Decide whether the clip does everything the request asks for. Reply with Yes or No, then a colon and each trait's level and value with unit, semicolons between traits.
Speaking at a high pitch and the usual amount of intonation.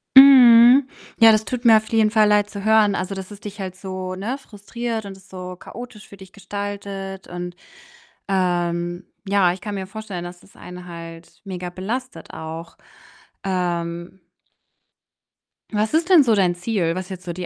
Yes: high, 195 Hz; average, 3.4 semitones